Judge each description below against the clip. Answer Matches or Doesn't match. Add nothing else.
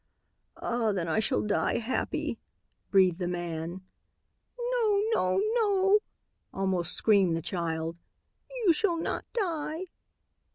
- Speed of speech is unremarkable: Doesn't match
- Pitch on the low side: Doesn't match